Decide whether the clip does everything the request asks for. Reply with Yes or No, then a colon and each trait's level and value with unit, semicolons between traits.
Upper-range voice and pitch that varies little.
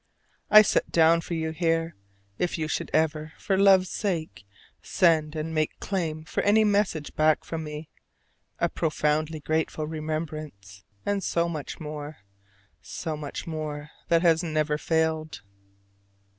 No: medium, 160 Hz; narrow, 1.6 semitones